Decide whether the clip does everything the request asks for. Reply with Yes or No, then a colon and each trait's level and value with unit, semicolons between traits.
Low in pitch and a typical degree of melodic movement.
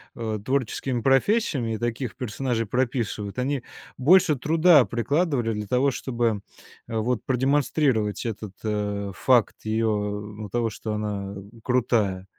Yes: low, 115 Hz; average, 3.9 semitones